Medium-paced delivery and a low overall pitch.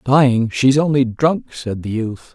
Yes: average, 180 wpm; low, 125 Hz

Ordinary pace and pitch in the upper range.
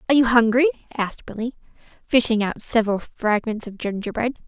Yes: average, 150 wpm; high, 230 Hz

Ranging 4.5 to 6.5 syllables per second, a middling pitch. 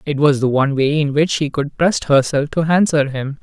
Yes: 5.3 syllables/s; medium, 145 Hz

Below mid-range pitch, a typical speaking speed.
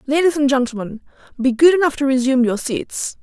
No: very high, 270 Hz; average, 185 wpm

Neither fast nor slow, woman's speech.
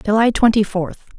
Yes: average, 150 wpm; female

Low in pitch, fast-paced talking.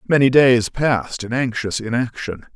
No: low, 120 Hz; average, 140 wpm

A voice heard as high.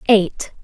Yes: high, 205 Hz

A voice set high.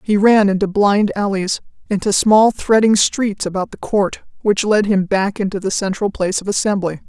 Yes: high, 200 Hz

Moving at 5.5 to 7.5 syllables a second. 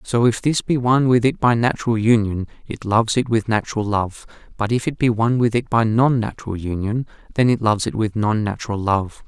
Yes: 5.9 syllables/s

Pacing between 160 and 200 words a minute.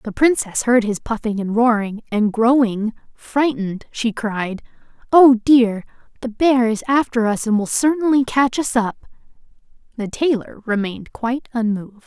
No: average, 150 wpm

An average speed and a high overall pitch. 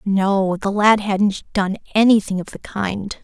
Yes: average, 165 wpm; high, 200 Hz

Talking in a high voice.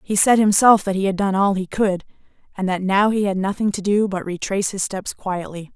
Yes: high, 195 Hz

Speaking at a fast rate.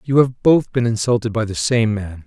Yes: fast, 240 wpm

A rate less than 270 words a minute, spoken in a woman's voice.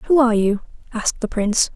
Yes: fast, 205 wpm; female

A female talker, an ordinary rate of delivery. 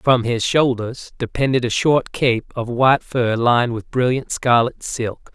No: male; average, 170 wpm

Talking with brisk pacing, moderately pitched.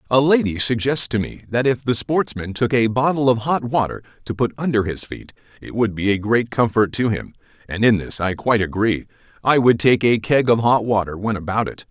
No: fast, 225 wpm; low, 115 Hz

